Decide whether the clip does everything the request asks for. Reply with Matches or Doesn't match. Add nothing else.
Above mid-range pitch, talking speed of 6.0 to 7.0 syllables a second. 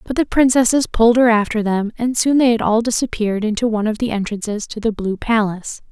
Matches